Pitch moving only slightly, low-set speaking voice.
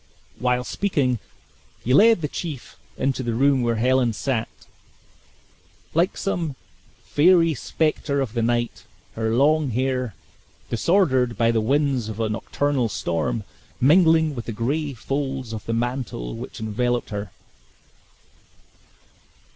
No: average, 4.0 semitones; low, 125 Hz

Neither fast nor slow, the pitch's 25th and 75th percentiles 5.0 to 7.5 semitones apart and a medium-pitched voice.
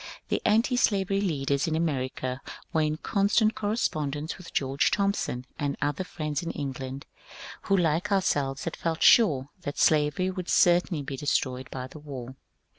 Yes: average, 155 wpm; average, 5.3 semitones; medium, 155 Hz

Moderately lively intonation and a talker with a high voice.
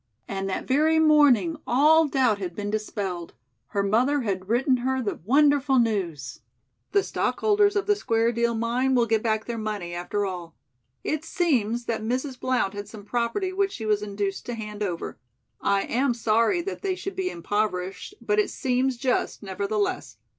No: wide, 5.7 semitones; high, 235 Hz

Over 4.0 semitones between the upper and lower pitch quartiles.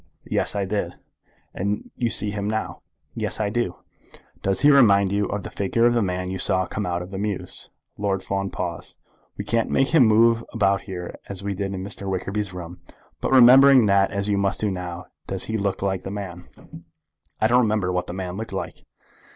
No: narrow, 2.4 semitones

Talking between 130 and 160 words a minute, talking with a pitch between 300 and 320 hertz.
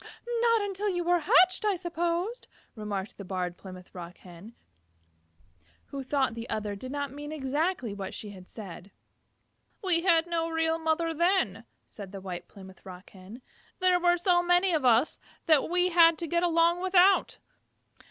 No: average, 170 wpm; very high, 315 Hz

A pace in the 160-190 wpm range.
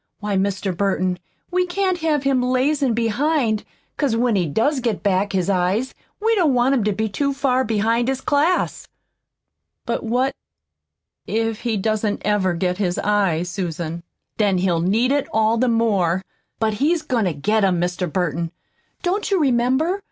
Yes: average, 165 wpm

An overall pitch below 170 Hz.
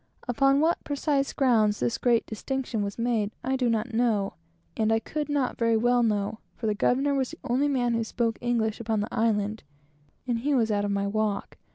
No: high, 230 Hz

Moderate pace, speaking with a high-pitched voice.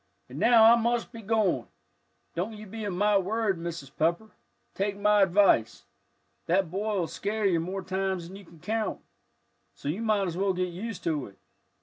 Yes: average, 190 wpm; high, 195 Hz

